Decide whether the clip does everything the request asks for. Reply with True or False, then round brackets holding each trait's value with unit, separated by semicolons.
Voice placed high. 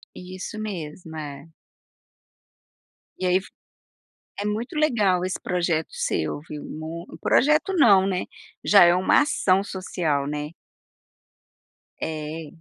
False (180 Hz)